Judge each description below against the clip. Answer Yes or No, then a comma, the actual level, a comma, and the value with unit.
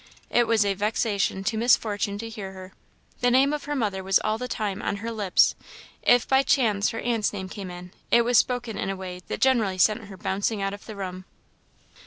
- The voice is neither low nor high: No, high, 210 Hz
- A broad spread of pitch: No, average, 3.3 semitones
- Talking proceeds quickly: Yes, fast, 225 wpm